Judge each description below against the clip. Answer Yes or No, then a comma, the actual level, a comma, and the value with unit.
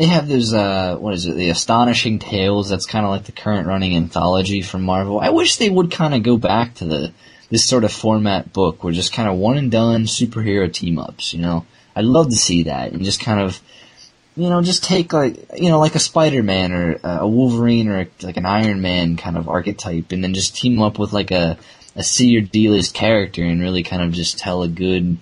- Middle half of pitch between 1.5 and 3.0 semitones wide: No, average, 4.6 semitones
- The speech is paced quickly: Yes, fast, 235 wpm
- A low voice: Yes, low, 100 Hz